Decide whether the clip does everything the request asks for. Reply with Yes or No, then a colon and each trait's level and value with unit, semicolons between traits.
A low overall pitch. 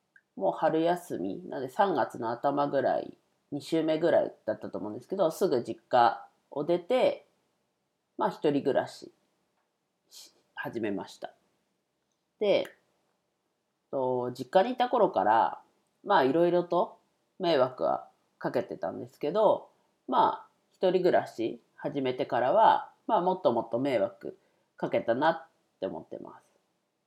No: medium, 170 Hz